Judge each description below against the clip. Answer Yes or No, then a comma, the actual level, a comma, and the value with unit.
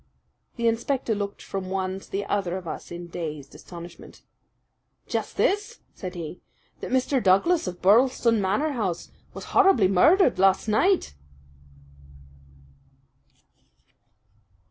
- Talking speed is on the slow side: Yes, slow, 120 wpm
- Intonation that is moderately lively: No, wide, 6.0 semitones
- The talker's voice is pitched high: Yes, high, 200 Hz